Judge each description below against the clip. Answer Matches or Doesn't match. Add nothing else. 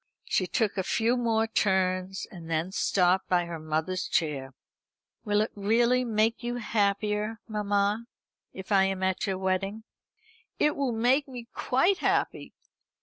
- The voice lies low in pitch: Doesn't match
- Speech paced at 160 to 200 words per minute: Doesn't match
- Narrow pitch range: Doesn't match